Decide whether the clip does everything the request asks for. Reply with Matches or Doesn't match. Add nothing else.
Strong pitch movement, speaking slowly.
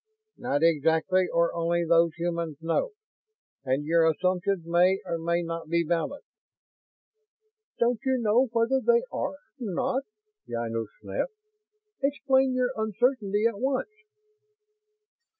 Matches